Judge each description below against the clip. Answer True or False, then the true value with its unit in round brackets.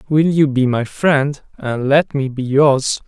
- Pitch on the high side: False (140 Hz)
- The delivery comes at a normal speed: True (195 wpm)